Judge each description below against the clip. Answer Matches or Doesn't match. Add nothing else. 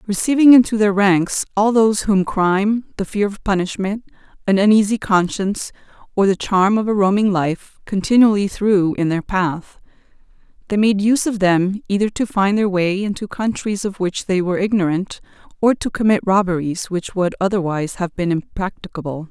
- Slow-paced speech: Doesn't match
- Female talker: Matches